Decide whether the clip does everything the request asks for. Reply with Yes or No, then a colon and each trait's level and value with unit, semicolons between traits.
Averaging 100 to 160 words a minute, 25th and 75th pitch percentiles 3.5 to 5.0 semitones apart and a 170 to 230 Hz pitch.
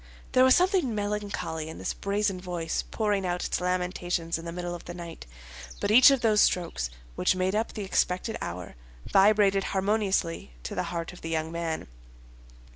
No: average, 180 wpm; average, 3.8 semitones; medium, 185 Hz